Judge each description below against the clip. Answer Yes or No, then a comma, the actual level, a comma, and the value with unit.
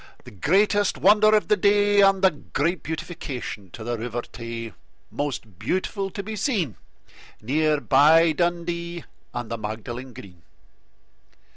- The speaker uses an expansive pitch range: Yes, wide, 8.4 semitones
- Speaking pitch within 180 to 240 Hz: No, medium, 160 Hz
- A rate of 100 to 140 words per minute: Yes, slow, 135 wpm